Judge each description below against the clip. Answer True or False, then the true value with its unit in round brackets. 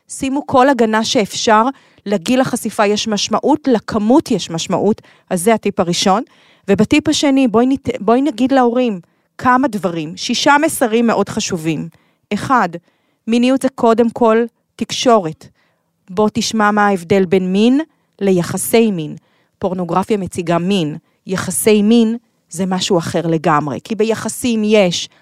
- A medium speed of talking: True (130 wpm)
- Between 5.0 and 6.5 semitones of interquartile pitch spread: False (4.4 semitones)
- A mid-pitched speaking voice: False (215 Hz)